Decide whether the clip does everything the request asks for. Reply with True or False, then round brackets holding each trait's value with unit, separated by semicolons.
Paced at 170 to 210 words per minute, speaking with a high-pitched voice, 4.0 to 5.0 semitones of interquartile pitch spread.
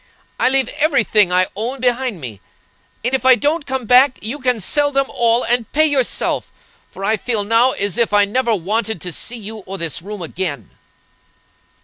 True (195 wpm; 230 Hz; 4.3 semitones)